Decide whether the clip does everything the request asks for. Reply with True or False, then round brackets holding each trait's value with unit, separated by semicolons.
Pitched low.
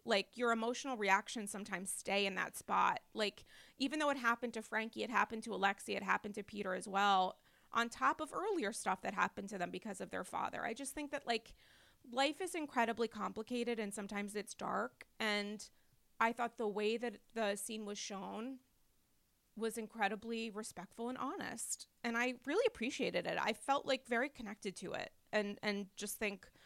False (225 Hz)